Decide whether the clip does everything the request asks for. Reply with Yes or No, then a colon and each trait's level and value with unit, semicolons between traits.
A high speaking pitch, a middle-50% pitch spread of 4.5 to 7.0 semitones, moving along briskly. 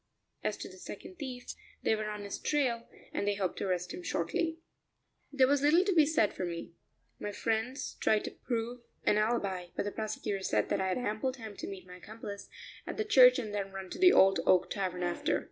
Yes: high, 215 Hz; average, 4.9 semitones; fast, 220 wpm